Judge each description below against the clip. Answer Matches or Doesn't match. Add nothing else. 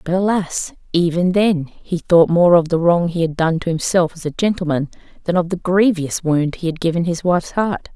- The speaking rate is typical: Doesn't match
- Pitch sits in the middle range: Matches